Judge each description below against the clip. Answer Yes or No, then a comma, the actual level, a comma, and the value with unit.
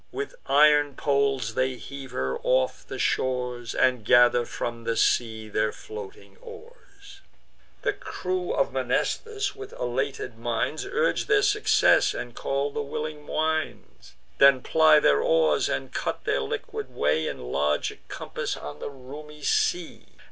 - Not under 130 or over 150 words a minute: Yes, average, 140 wpm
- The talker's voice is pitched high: No, medium, 140 Hz